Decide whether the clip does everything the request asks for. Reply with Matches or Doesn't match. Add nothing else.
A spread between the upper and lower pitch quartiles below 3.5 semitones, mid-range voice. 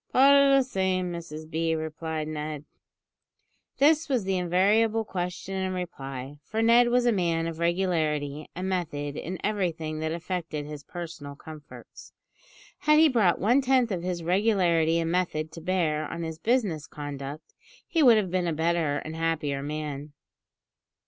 Doesn't match